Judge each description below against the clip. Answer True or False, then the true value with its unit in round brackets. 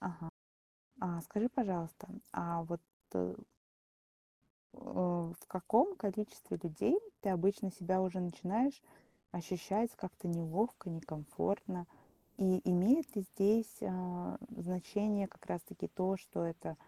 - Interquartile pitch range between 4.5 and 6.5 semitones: False (3.2 semitones)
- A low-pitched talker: False (185 Hz)